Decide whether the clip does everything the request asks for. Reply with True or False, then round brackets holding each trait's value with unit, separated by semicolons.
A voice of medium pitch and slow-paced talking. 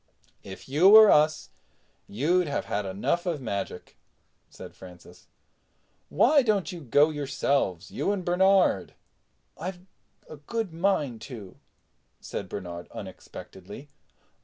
True (150 Hz; 110 wpm)